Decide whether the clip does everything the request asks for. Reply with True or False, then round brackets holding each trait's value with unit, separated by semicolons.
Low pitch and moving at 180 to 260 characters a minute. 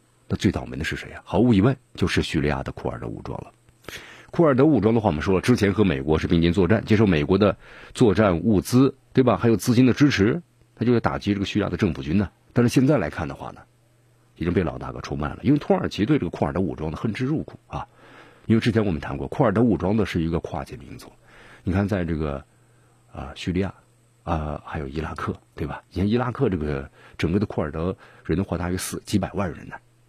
False (105 Hz; 360 characters per minute)